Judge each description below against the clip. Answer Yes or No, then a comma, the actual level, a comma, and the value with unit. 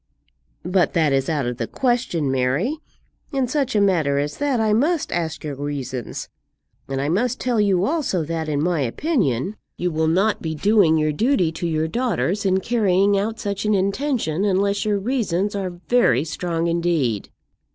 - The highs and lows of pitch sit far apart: Yes, wide, 5.9 semitones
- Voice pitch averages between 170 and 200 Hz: Yes, medium, 185 Hz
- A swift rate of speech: No, average, 175 wpm